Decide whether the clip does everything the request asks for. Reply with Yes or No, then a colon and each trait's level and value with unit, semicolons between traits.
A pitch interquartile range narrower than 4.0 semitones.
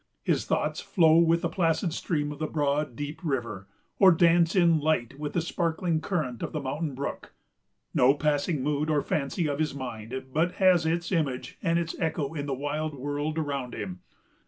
Yes: average, 2.9 semitones